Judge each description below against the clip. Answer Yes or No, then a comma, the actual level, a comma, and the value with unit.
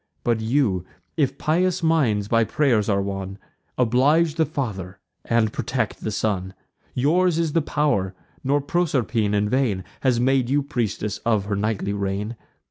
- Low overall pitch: Yes, low, 115 Hz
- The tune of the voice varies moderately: No, wide, 6.0 semitones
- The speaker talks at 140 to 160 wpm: Yes, average, 150 wpm